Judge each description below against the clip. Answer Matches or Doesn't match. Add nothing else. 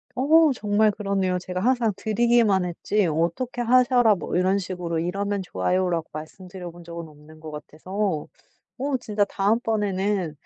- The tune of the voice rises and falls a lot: Doesn't match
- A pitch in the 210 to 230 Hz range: Doesn't match